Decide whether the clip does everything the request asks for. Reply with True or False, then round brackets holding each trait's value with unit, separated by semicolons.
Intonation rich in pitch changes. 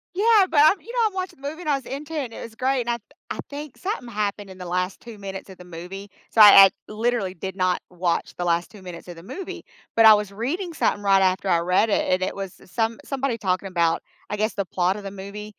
True (5.8 semitones)